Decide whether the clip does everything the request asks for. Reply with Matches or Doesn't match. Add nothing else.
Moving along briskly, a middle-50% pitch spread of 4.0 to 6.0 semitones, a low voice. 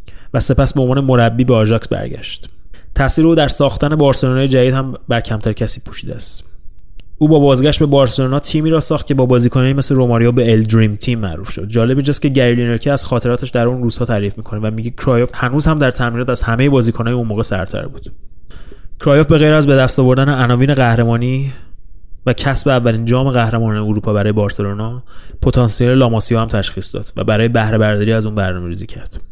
Doesn't match